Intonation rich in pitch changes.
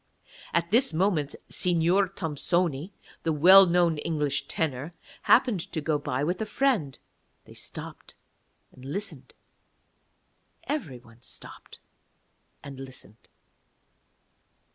No: average, 4.8 semitones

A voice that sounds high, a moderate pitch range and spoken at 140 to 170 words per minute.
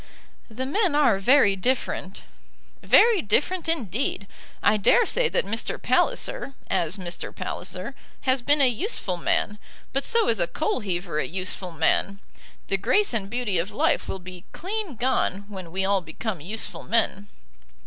No: high, 215 Hz; wide, 6.7 semitones; average, 160 wpm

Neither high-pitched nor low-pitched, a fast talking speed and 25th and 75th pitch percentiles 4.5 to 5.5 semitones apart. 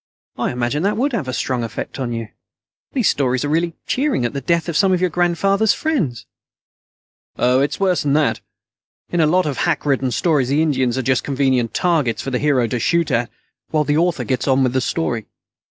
Yes: medium, 145 Hz; fast, 215 wpm; average, 5.2 semitones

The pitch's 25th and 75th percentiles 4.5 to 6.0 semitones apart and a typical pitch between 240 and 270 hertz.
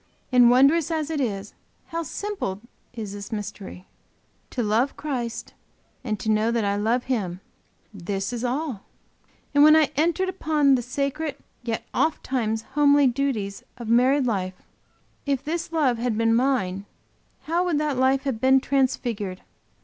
Yes: average, 4.8 semitones; very high, 250 Hz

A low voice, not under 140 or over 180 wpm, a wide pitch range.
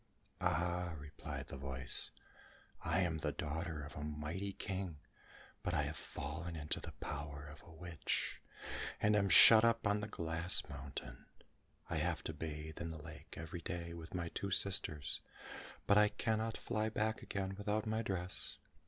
No: very low, 85 Hz; average, 165 wpm; average, 4.7 semitones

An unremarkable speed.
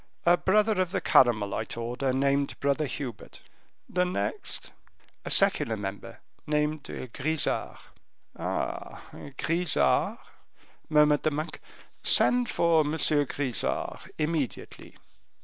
No: slow, 100 wpm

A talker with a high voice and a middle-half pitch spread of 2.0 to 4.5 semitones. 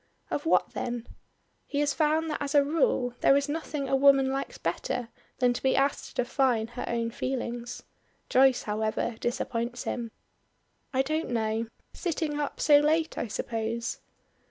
Yes: very high, 265 Hz; average, 3.6 semitones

